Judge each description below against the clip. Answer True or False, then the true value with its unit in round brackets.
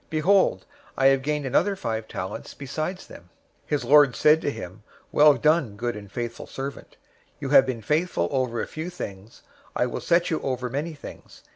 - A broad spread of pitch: False (4.7 semitones)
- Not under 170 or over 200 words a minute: True (185 wpm)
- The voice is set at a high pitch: False (135 Hz)